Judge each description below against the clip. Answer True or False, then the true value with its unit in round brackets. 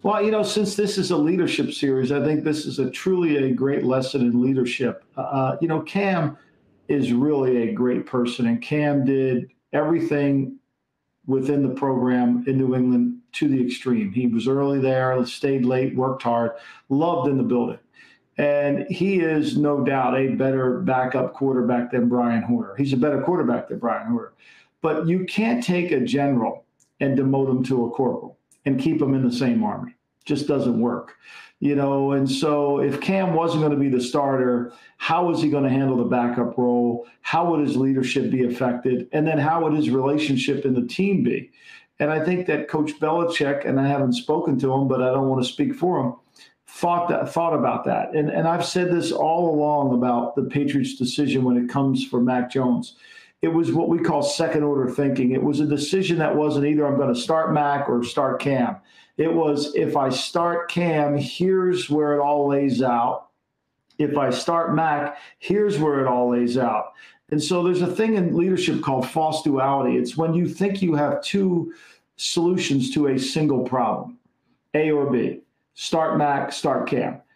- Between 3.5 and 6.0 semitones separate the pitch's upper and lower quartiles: True (4.0 semitones)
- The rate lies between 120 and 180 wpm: False (190 wpm)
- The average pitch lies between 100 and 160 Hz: True (140 Hz)